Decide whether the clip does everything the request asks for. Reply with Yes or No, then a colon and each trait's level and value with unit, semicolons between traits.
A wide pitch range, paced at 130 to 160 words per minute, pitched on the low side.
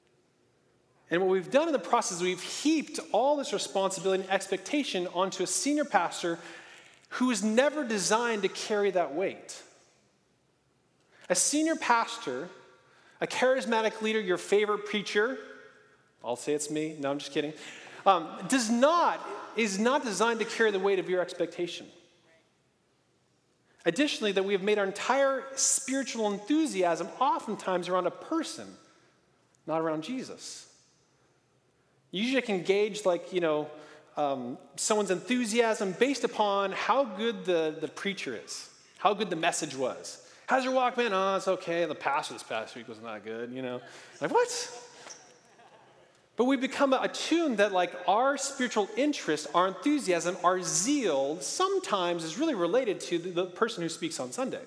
No: wide, 6.5 semitones; average, 155 wpm; high, 200 Hz